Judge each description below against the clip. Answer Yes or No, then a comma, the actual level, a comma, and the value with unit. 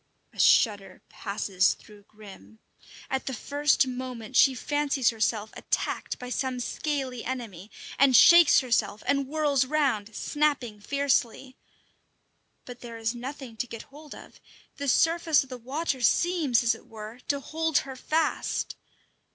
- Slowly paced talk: No, average, 145 wpm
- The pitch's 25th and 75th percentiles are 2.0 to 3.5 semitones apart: No, average, 4.0 semitones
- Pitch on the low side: No, very high, 255 Hz